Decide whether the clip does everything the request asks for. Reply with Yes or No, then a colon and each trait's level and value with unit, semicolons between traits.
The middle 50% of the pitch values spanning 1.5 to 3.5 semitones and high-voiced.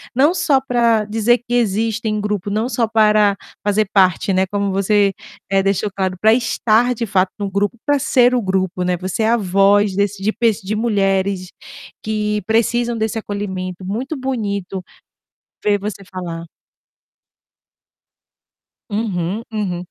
Yes: narrow, 2.6 semitones; high, 210 Hz